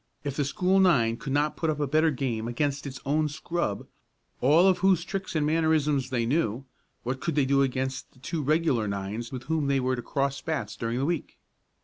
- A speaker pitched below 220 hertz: Yes, medium, 140 Hz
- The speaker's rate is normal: No, fast, 215 wpm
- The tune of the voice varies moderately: Yes, average, 3.7 semitones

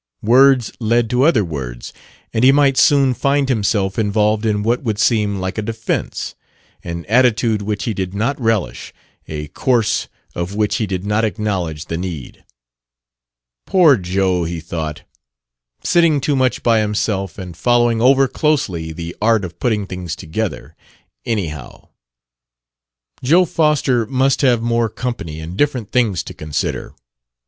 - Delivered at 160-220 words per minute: No, average, 145 wpm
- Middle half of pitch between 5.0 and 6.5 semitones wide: Yes, average, 5.3 semitones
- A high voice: No, low, 110 Hz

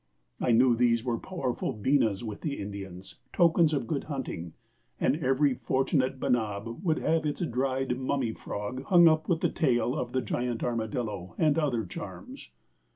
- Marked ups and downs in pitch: No, average, 4.6 semitones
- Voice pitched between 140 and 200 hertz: No, low, 130 Hz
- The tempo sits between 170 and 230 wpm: No, average, 160 wpm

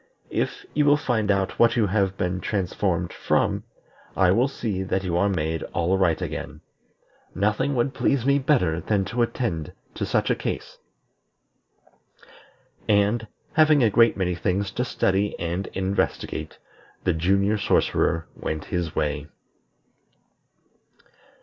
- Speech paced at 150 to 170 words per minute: No, slow, 135 wpm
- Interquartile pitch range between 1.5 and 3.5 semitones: No, average, 4.7 semitones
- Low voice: Yes, low, 100 Hz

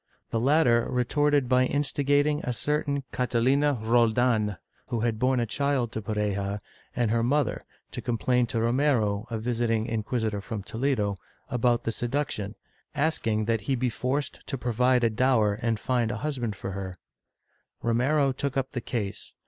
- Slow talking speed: No, average, 155 wpm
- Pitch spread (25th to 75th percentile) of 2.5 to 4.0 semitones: Yes, average, 3.3 semitones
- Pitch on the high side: No, low, 120 Hz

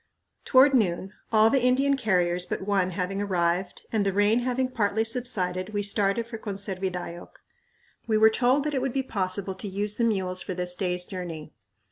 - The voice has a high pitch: Yes, high, 200 Hz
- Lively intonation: No, average, 4.1 semitones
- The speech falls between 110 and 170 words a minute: No, average, 180 wpm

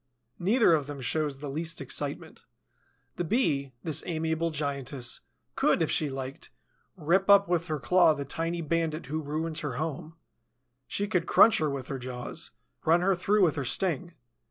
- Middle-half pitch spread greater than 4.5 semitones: No, average, 3.6 semitones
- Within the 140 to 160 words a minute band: No, average, 170 wpm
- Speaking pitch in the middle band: Yes, medium, 160 Hz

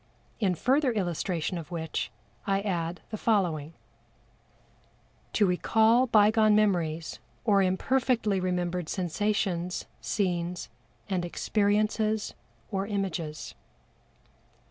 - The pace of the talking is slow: Yes, slow, 90 wpm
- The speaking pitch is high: Yes, high, 195 Hz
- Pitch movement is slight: No, average, 3.5 semitones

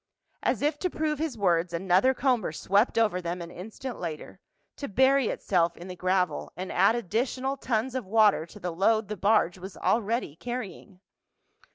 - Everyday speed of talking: Yes, average, 175 wpm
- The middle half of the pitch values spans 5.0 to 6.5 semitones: Yes, wide, 5.6 semitones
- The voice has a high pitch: Yes, high, 210 Hz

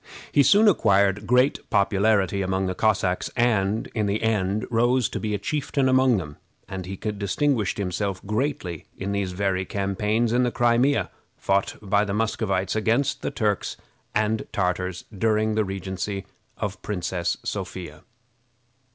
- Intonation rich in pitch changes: No, average, 3.0 semitones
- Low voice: Yes, low, 105 Hz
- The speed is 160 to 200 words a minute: No, average, 150 wpm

